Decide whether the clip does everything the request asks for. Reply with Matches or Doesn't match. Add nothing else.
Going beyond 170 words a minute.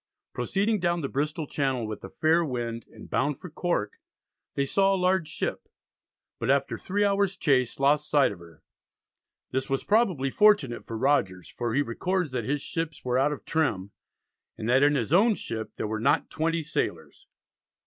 Matches